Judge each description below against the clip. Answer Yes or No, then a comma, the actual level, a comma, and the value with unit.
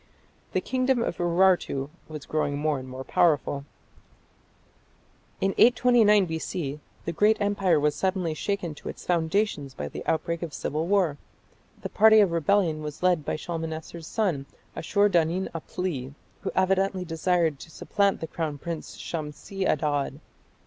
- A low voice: No, medium, 170 Hz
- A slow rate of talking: No, average, 145 wpm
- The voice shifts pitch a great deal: No, average, 4.1 semitones